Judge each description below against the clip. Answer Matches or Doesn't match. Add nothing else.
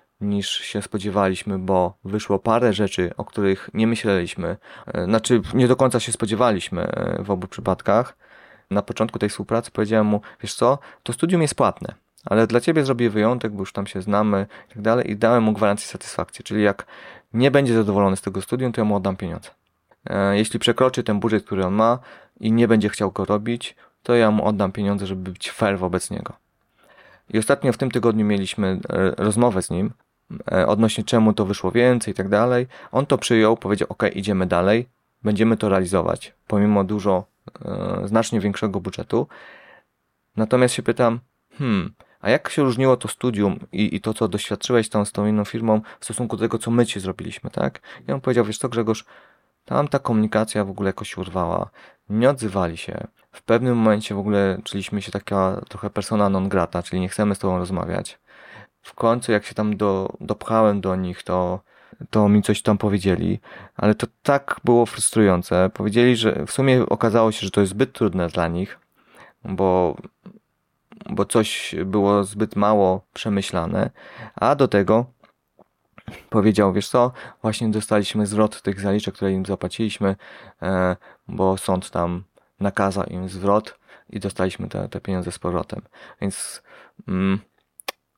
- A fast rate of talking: Matches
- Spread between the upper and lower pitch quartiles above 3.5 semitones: Doesn't match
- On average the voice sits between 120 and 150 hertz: Doesn't match